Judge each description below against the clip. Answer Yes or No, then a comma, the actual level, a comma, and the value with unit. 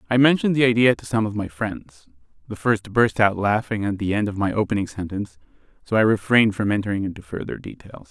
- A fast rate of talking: Yes, fast, 215 wpm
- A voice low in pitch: Yes, low, 105 Hz